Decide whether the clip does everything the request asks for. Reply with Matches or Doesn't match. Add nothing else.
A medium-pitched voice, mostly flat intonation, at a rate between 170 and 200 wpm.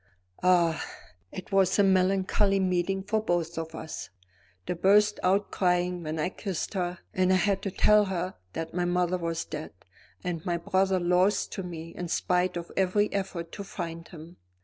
Matches